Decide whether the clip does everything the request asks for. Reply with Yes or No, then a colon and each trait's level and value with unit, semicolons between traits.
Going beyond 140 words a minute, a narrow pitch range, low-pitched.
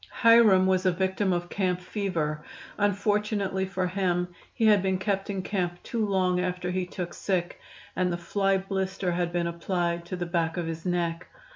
No: average, 180 wpm; narrow, 1.9 semitones; medium, 185 Hz